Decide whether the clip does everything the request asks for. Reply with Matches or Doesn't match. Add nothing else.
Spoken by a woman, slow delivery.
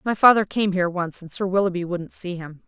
Doesn't match